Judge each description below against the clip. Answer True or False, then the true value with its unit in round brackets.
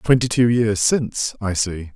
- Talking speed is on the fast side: False (185 wpm)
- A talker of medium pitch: False (110 Hz)